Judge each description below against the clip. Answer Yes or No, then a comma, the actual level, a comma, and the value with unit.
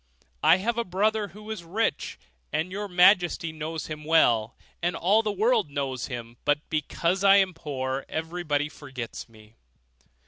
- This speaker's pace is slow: No, average, 160 wpm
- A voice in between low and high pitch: Yes, medium, 165 Hz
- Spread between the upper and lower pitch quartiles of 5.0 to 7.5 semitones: Yes, wide, 5.4 semitones